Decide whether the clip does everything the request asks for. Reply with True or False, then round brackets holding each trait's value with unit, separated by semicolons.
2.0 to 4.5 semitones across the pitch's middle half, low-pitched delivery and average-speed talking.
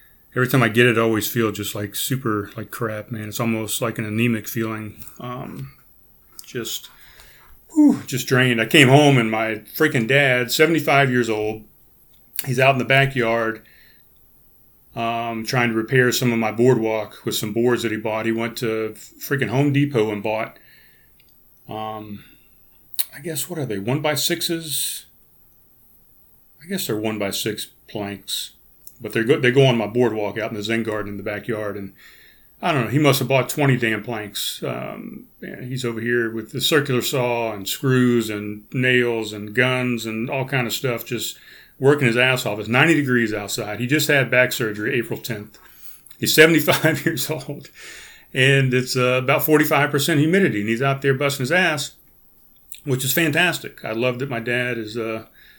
True (3.6 semitones; 120 Hz; 185 wpm)